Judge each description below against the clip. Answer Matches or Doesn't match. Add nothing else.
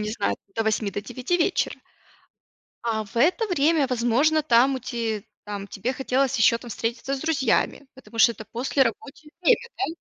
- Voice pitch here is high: Matches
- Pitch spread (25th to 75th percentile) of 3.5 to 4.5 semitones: Matches